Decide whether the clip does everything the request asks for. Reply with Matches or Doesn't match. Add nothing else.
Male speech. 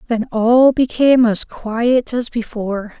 Doesn't match